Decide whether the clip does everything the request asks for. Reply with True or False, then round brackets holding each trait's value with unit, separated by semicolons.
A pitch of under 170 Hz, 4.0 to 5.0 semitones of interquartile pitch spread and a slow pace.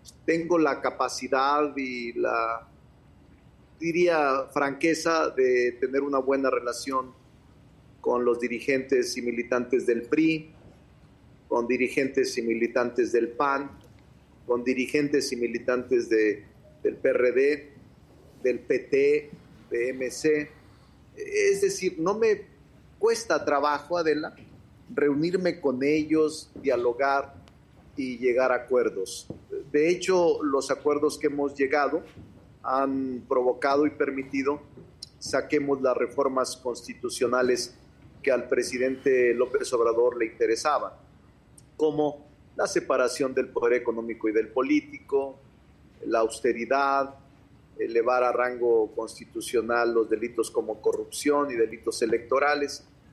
True (140 Hz; 4.7 semitones; 105 wpm)